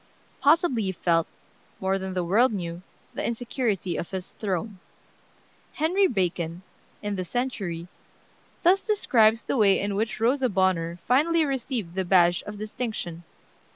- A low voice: No, high, 205 Hz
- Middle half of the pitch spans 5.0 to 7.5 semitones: Yes, wide, 5.6 semitones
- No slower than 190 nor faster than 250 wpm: No, average, 140 wpm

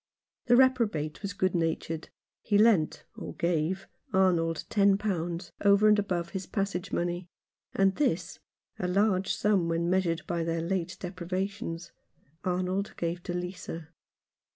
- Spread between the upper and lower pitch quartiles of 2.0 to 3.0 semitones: Yes, average, 2.7 semitones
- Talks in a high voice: No, medium, 180 Hz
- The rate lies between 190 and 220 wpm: No, average, 155 wpm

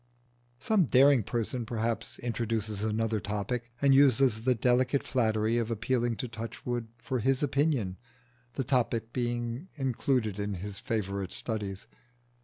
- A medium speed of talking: No, slow, 130 wpm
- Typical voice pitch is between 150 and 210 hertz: No, low, 115 Hz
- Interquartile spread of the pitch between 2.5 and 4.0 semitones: Yes, average, 2.9 semitones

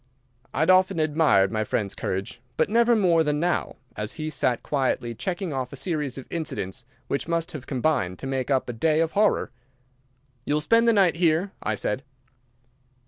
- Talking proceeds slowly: No, average, 190 wpm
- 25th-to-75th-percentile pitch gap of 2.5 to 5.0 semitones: No, wide, 5.4 semitones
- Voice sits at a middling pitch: Yes, medium, 150 Hz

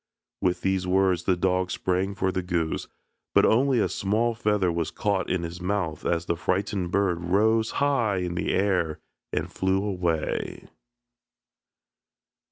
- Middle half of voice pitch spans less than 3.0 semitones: Yes, narrow, 2.6 semitones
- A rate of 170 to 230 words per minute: No, average, 150 wpm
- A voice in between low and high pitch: No, very low, 95 Hz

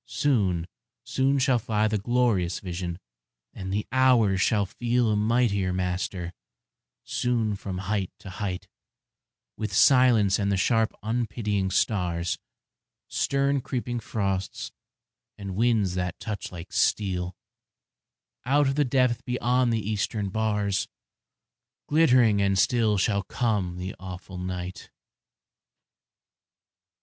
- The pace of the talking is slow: Yes, slow, 115 wpm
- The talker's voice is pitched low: Yes, low, 105 Hz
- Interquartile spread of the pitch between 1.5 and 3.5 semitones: No, average, 4.3 semitones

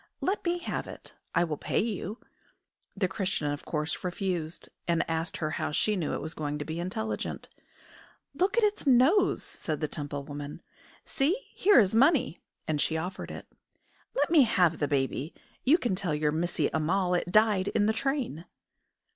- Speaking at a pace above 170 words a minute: Yes, average, 180 wpm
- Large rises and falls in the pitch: Yes, wide, 7.1 semitones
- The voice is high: No, medium, 180 Hz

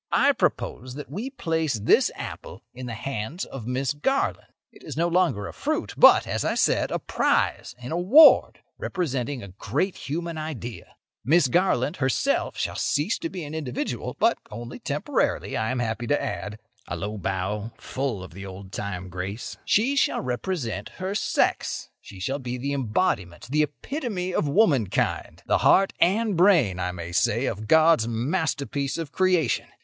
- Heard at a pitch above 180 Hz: No, low, 135 Hz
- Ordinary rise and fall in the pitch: No, wide, 7.8 semitones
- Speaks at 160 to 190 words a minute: Yes, average, 165 wpm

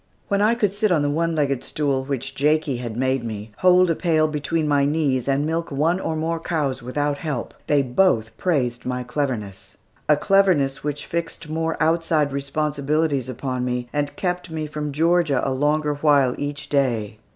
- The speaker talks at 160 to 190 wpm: Yes, average, 180 wpm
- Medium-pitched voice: Yes, medium, 145 Hz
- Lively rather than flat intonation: No, average, 3.5 semitones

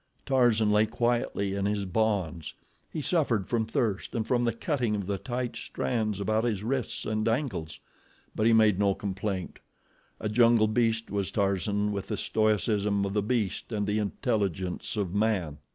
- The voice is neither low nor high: No, low, 105 Hz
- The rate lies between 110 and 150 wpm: No, average, 170 wpm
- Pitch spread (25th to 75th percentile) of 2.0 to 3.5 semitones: Yes, narrow, 2.5 semitones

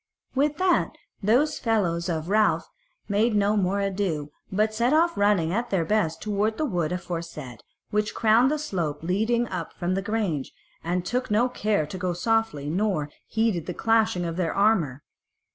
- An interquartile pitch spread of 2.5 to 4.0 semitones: No, average, 4.7 semitones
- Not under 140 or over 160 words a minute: No, average, 175 wpm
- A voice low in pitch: No, high, 200 Hz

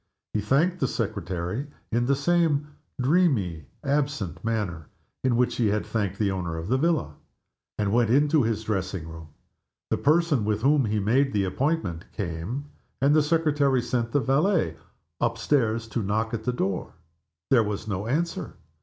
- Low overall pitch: Yes, low, 115 Hz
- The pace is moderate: Yes, average, 170 wpm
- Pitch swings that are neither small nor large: No, wide, 5.9 semitones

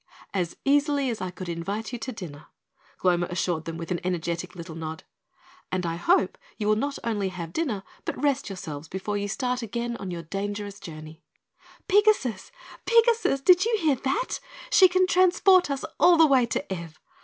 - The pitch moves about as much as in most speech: No, wide, 8.5 semitones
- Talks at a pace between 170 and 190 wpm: Yes, average, 180 wpm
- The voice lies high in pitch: Yes, high, 205 Hz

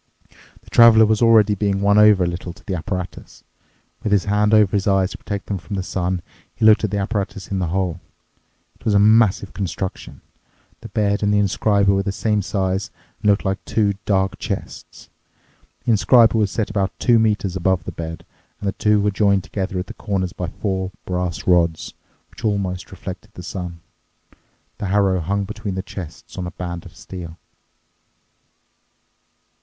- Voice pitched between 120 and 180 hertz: No, low, 100 Hz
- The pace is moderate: Yes, average, 185 wpm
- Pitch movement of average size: No, narrow, 2.2 semitones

